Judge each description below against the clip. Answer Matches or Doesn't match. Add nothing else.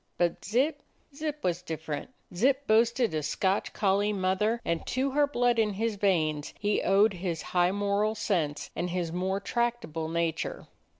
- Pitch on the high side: Matches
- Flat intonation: Doesn't match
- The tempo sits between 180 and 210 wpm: Doesn't match